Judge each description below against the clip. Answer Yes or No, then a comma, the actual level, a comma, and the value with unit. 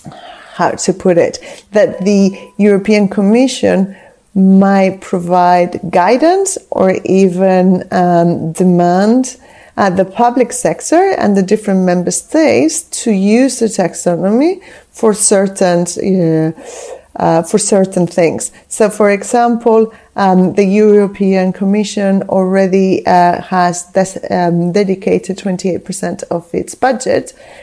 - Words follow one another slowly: Yes, slow, 120 wpm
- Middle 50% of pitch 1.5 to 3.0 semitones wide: No, average, 3.6 semitones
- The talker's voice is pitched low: No, high, 195 Hz